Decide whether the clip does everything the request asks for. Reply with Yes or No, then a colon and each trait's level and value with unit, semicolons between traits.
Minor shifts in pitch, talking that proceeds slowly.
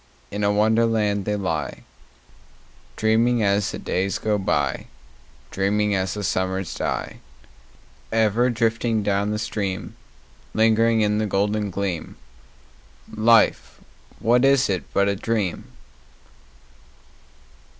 Yes: narrow, 2.3 semitones; slow, 110 wpm